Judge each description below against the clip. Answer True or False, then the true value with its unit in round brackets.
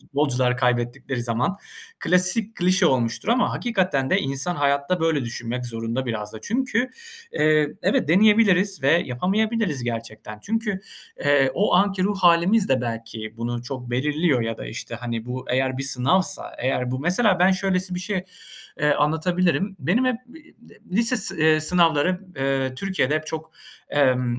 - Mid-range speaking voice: True (150 Hz)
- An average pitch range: False (6.9 semitones)